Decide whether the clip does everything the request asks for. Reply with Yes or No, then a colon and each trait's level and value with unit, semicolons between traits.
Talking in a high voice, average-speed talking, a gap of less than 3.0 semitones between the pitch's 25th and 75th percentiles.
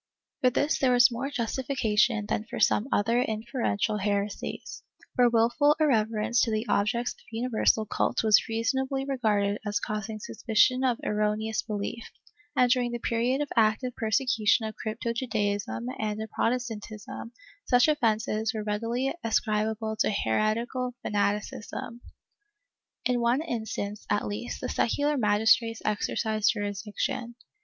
No: high, 225 Hz; slow, 130 wpm; narrow, 2.6 semitones